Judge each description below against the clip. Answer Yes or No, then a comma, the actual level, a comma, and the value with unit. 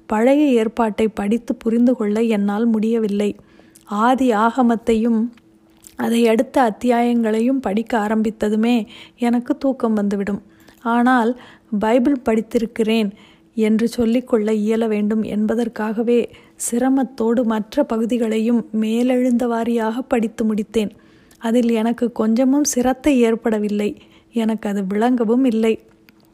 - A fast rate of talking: No, average, 90 wpm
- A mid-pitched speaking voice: No, high, 230 Hz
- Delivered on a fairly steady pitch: Yes, narrow, 1.8 semitones